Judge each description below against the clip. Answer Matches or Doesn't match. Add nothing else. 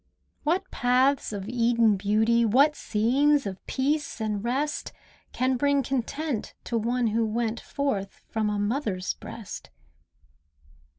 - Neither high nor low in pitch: Doesn't match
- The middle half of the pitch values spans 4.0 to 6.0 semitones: Matches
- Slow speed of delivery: Matches